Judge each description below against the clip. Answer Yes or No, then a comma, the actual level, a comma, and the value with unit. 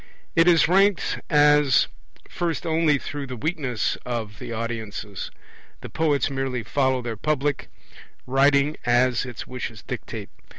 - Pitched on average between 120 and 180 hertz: Yes, low, 135 Hz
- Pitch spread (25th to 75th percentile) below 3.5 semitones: No, average, 3.8 semitones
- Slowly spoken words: Yes, slow, 130 wpm